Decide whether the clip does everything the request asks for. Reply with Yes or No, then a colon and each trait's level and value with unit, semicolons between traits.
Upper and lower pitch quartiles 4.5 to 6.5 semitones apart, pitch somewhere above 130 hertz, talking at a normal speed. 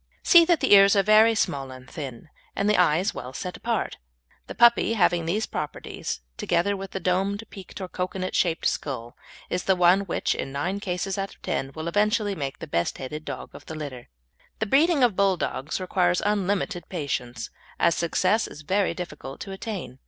Yes: average, 4.8 semitones; medium, 185 Hz; average, 190 wpm